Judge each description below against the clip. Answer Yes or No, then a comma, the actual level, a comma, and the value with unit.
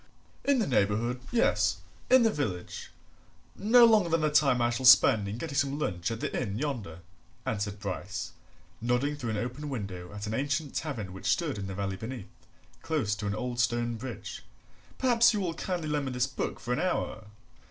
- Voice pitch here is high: No, low, 125 Hz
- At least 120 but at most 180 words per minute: No, average, 195 wpm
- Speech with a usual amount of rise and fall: No, wide, 6.3 semitones